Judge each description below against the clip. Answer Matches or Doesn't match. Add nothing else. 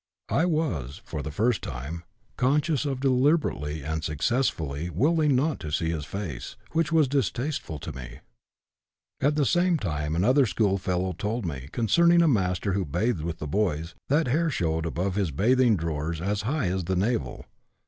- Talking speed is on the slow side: Doesn't match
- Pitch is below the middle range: Matches